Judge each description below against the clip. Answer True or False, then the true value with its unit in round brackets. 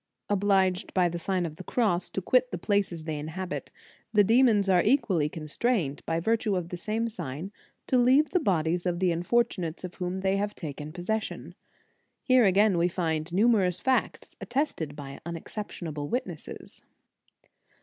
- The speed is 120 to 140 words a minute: False (165 wpm)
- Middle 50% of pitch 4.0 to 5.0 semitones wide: True (4.5 semitones)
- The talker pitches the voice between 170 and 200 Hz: True (185 Hz)